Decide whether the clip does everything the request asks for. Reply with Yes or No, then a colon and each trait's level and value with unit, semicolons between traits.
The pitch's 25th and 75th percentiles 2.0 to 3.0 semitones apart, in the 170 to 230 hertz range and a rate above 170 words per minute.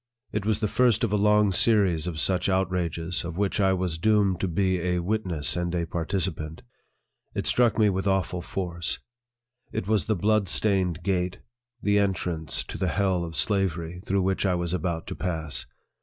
No: average, 2.7 semitones; very low, 95 Hz; average, 185 wpm